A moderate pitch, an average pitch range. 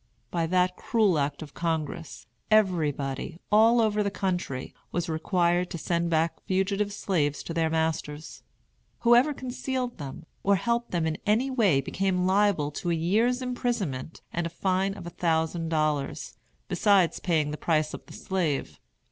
Yes: medium, 175 Hz; average, 4.4 semitones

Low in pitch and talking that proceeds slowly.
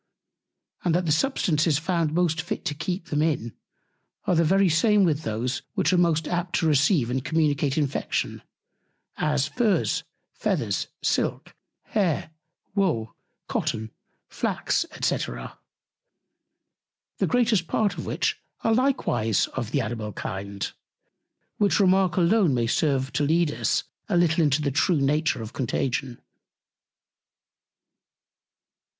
No: medium, 155 Hz; slow, 130 wpm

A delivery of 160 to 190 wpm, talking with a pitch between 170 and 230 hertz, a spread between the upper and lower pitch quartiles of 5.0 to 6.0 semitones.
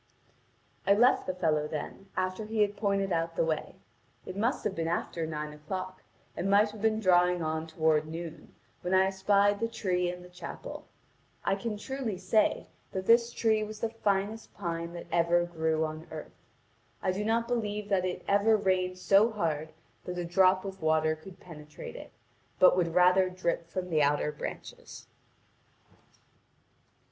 No: average, 170 wpm; medium, 185 Hz; average, 3.6 semitones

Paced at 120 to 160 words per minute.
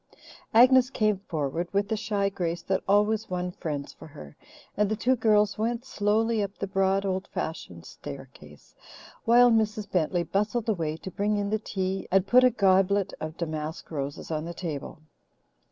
No: average, 170 wpm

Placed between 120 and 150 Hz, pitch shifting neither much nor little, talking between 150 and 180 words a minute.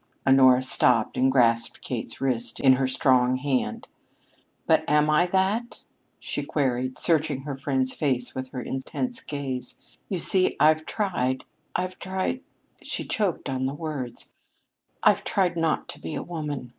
Yes: low, 135 Hz; average, 4.0 semitones; average, 155 wpm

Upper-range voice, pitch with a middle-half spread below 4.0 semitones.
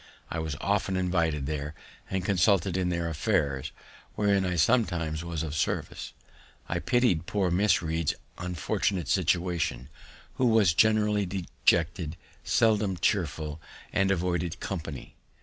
No: very low, 90 Hz; average, 3.4 semitones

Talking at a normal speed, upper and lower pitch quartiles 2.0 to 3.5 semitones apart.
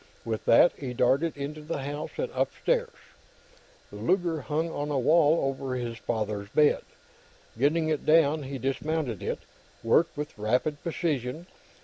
No: average, 145 wpm; average, 4.0 semitones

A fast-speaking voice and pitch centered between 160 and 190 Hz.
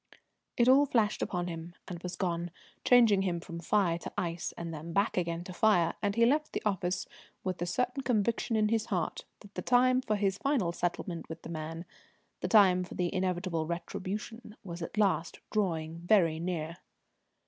No: average, 185 wpm; medium, 185 Hz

